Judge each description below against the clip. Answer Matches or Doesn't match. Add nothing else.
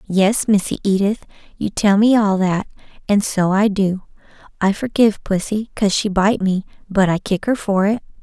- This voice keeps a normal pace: Matches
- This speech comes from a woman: Matches